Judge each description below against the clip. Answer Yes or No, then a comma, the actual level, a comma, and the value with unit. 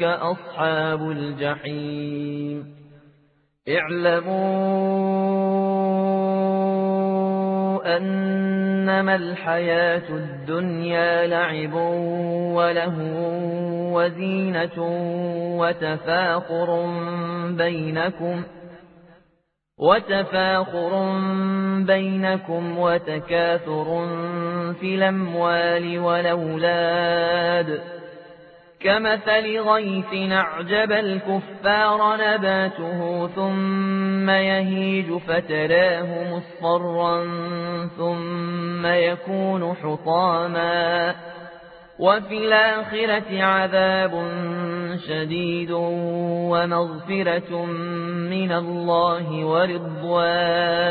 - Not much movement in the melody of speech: Yes, narrow, 2.0 semitones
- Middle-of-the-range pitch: Yes, medium, 175 Hz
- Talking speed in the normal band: No, slow, 45 wpm